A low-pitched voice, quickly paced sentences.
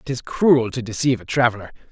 Yes: low, 120 Hz; fast, 220 wpm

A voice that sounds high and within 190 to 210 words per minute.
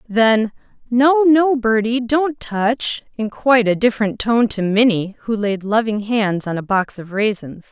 No: high, 225 Hz; average, 170 wpm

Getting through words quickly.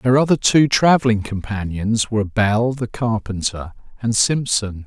No: slow, 135 wpm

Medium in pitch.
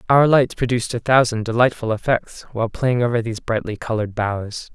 No: low, 115 Hz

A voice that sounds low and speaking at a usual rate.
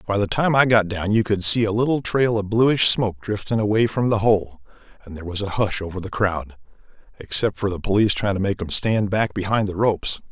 No: low, 105 Hz; fast, 240 wpm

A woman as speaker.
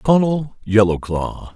No: male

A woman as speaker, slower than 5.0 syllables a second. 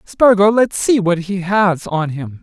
No: male; 3.9 syllables/s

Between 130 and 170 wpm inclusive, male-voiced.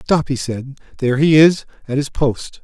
No: fast, 205 wpm; male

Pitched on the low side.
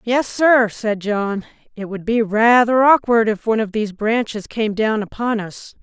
No: high, 220 Hz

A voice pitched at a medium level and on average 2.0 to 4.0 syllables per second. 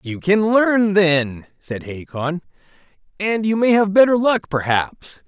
Yes: medium, 180 Hz; 3.7 syllables/s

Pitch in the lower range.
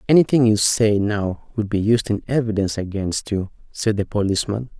Yes: low, 105 Hz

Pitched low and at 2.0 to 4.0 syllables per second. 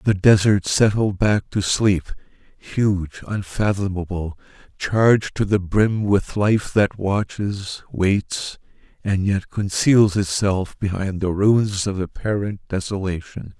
Yes: low, 100 Hz; 3.7 syllables/s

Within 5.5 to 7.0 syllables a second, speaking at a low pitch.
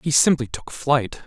No: 4.1 syllables/s; low, 130 Hz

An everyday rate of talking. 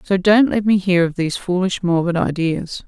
No: fast, 210 wpm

